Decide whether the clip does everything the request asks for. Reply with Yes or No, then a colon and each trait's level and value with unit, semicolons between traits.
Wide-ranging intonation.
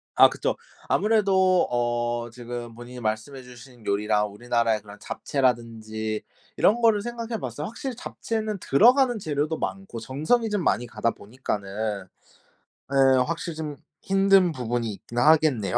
Yes: wide, 8.7 semitones